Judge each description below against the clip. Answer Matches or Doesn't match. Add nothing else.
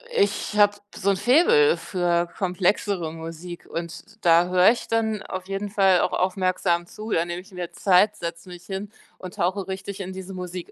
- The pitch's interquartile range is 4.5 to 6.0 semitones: Doesn't match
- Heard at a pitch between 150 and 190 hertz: Matches